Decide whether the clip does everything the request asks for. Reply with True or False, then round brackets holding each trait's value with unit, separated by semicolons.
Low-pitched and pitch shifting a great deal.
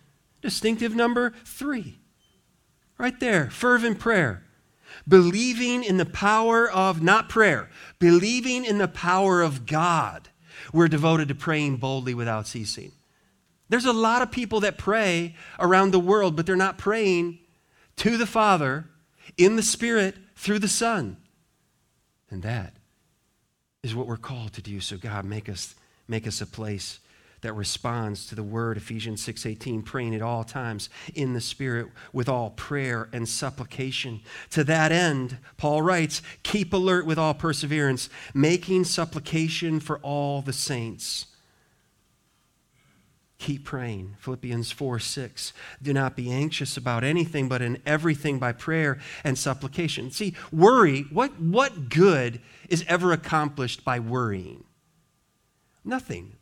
False (150 Hz; 7.6 semitones)